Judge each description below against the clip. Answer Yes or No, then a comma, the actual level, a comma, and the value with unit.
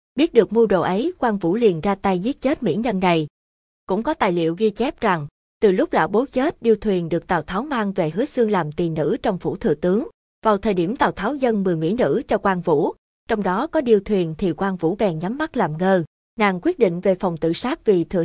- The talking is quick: Yes, fast, 255 wpm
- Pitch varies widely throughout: No, average, 4.8 semitones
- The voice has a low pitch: No, high, 205 Hz